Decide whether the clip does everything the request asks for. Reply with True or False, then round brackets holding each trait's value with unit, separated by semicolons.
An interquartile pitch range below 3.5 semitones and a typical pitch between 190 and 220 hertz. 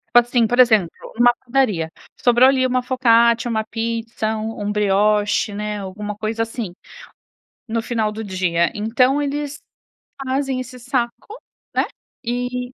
False (2.9 semitones; 230 Hz)